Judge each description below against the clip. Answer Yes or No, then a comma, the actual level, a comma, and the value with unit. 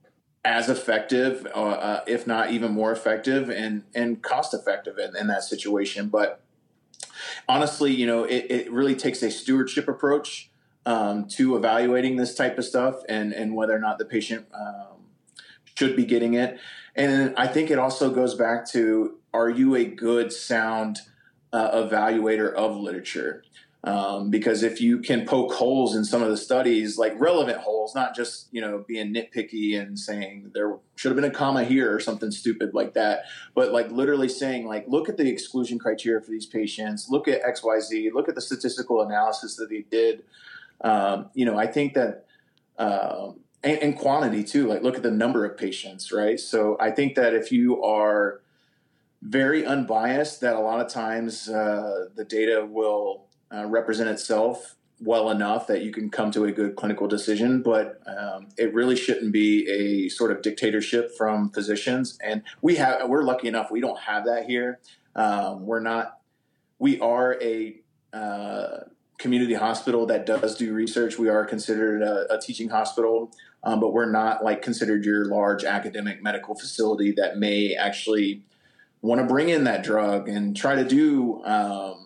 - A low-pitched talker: Yes, low, 115 Hz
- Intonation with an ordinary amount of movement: Yes, average, 3.2 semitones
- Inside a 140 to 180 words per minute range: Yes, average, 175 wpm